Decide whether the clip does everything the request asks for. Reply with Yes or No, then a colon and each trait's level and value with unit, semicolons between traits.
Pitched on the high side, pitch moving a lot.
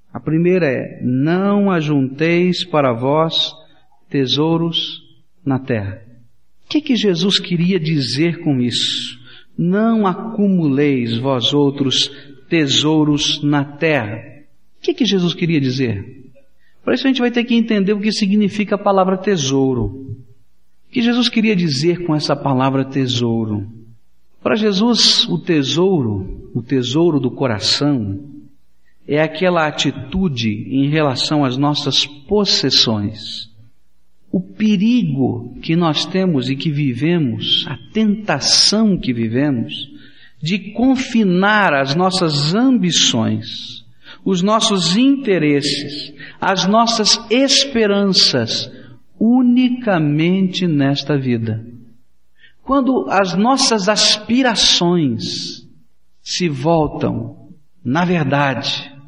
No: medium, 155 Hz; wide, 6.8 semitones